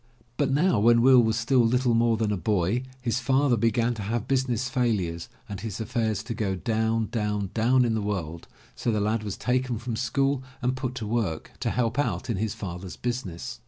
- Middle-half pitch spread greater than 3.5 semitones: No, average, 3.1 semitones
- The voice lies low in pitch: Yes, low, 115 Hz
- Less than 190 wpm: No, fast, 205 wpm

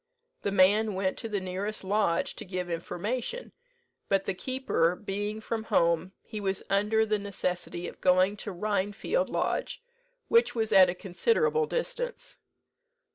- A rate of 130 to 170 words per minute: Yes, average, 145 wpm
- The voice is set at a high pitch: Yes, high, 205 Hz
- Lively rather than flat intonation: No, average, 3.0 semitones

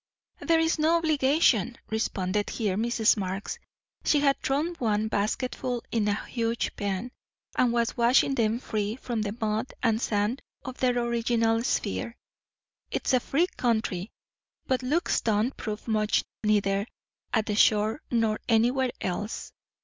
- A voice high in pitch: Yes, high, 230 Hz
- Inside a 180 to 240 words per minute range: No, average, 140 wpm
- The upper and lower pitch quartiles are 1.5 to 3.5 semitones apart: Yes, average, 3.2 semitones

